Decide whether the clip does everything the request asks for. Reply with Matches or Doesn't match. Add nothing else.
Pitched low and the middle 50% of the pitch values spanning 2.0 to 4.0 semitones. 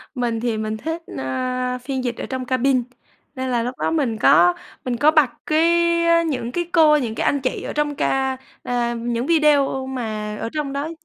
Doesn't match